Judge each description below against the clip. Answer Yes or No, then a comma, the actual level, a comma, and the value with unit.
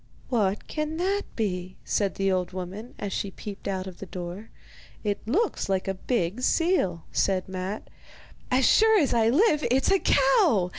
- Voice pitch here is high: Yes, high, 205 Hz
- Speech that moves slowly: No, average, 175 wpm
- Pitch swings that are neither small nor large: No, wide, 6.2 semitones